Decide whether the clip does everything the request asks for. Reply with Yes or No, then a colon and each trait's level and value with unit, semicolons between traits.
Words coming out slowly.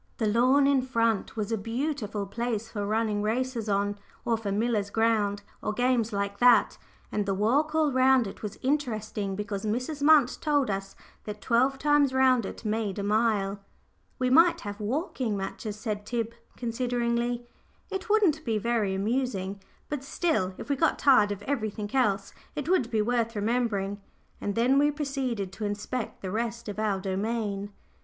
No: average, 170 wpm